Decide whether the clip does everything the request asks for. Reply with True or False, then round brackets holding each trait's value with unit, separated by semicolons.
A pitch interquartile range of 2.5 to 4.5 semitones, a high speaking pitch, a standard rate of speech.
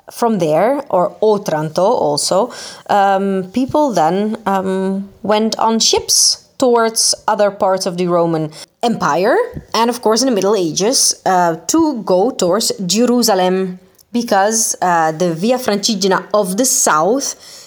True (4.2 semitones; 205 Hz; 130 wpm)